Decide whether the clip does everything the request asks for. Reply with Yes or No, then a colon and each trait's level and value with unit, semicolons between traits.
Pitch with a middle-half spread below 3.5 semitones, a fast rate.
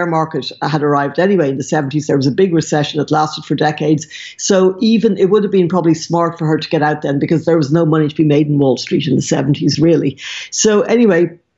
Yes: average, 2.7 semitones; fast, 245 wpm